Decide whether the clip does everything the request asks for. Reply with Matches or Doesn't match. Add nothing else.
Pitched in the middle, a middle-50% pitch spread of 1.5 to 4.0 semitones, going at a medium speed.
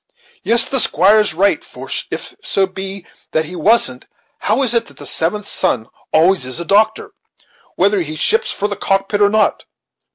Doesn't match